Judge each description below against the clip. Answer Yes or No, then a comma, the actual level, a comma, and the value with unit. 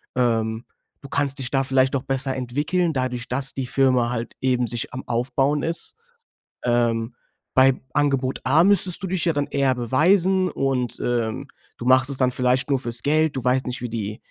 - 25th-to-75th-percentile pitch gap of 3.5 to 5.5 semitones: No, narrow, 2.6 semitones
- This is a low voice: Yes, low, 130 Hz